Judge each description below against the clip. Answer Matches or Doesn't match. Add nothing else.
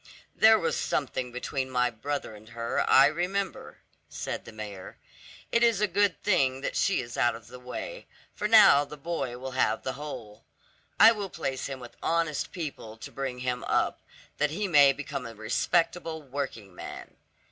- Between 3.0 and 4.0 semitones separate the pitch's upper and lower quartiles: Doesn't match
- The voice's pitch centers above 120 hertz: Matches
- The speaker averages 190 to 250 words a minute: Doesn't match